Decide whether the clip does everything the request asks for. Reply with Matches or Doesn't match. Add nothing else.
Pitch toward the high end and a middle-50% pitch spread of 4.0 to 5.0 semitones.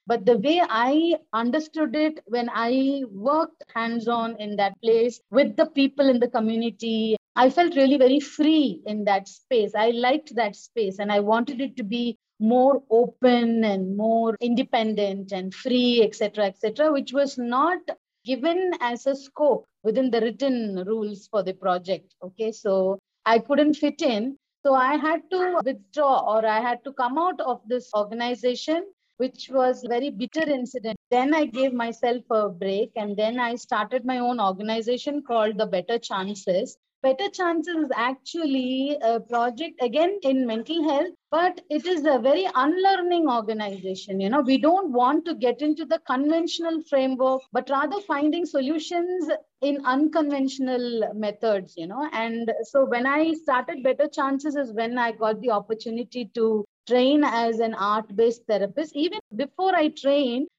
Matches